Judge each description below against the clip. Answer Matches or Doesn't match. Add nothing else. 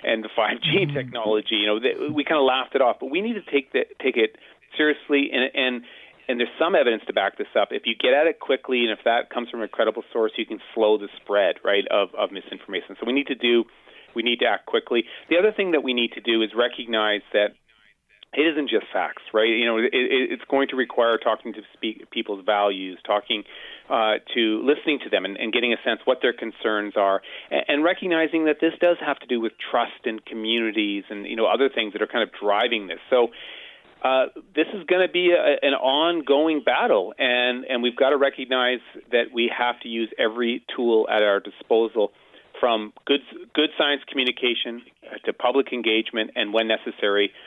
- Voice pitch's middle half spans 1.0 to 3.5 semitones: Doesn't match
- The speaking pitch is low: Matches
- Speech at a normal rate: Doesn't match